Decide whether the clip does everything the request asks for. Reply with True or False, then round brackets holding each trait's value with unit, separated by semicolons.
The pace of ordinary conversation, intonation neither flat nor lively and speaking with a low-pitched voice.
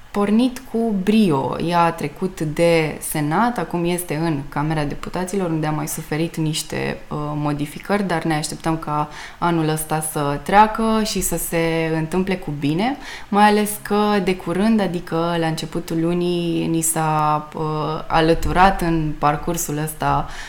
False (145 wpm; 3.2 semitones; 165 Hz)